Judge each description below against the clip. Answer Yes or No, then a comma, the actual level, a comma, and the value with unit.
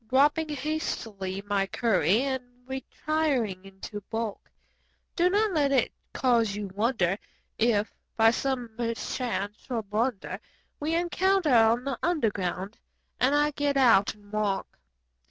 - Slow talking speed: Yes, slow, 125 wpm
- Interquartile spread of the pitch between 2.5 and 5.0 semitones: No, wide, 5.5 semitones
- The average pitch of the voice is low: No, high, 235 Hz